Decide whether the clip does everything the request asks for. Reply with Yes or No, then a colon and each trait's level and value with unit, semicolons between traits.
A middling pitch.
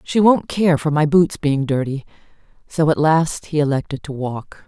Yes: medium, 150 Hz